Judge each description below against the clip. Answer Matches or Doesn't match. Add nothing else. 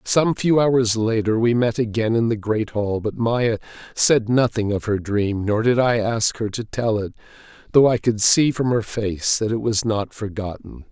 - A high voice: Doesn't match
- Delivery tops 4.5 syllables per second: Doesn't match